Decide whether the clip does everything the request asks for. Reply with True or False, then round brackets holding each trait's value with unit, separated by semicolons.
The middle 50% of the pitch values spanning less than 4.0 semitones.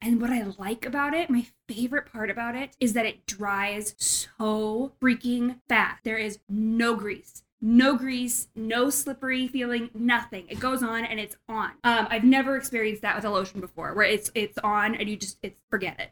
True (2.7 semitones)